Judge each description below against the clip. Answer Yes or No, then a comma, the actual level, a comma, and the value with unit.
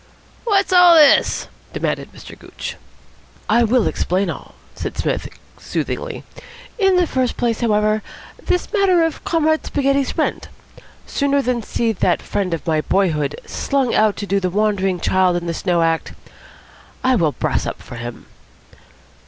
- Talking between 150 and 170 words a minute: Yes, average, 155 wpm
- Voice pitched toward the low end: No, high, 220 Hz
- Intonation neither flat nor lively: No, wide, 7.5 semitones